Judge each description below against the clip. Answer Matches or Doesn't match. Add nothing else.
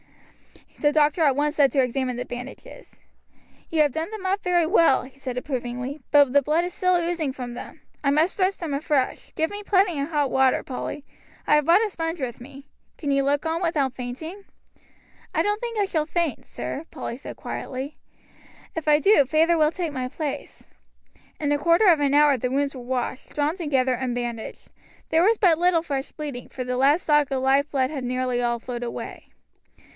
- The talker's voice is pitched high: Matches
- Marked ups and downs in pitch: Doesn't match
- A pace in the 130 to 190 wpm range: Doesn't match